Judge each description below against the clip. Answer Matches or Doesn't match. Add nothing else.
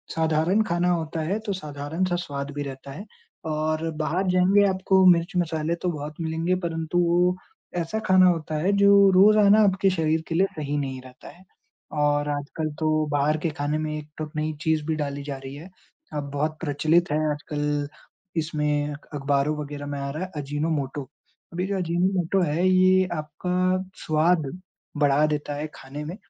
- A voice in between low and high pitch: Matches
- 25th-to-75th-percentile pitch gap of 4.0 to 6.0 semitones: Doesn't match